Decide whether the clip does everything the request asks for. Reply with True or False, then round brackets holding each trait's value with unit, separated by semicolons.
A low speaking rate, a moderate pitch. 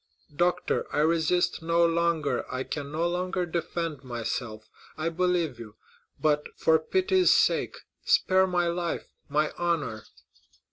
True (120 wpm; 165 Hz)